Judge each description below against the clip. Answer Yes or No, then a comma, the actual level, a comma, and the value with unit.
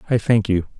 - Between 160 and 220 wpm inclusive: No, fast, 230 wpm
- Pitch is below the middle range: Yes, low, 105 Hz